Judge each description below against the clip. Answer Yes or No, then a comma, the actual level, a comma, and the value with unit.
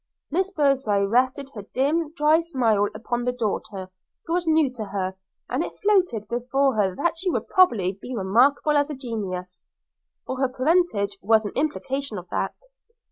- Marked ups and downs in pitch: Yes, wide, 6.5 semitones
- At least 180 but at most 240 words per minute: No, average, 165 wpm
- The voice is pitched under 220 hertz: No, very high, 255 Hz